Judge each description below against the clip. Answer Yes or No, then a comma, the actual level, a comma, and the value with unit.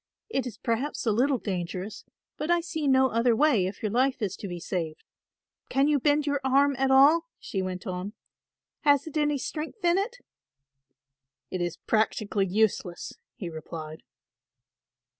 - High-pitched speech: Yes, high, 245 Hz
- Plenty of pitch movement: Yes, wide, 7.2 semitones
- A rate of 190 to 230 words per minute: No, average, 160 wpm